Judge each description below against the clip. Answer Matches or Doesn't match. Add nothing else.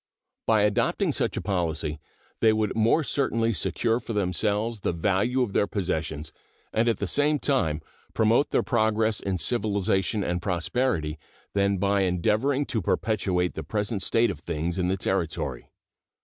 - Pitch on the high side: Doesn't match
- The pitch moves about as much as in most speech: Matches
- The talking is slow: Doesn't match